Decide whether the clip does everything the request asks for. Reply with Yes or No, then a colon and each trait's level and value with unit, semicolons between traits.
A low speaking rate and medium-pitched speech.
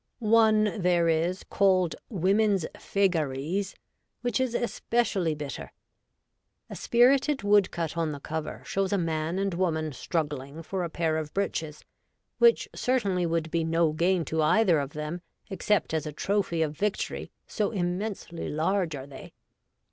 No: average, 145 wpm; medium, 175 Hz